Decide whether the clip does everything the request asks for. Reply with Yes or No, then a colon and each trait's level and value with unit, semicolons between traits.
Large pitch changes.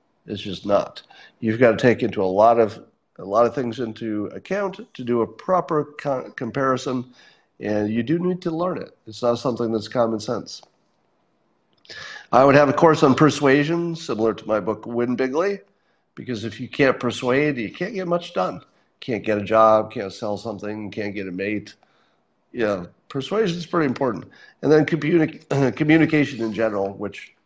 Yes: wide, 5.7 semitones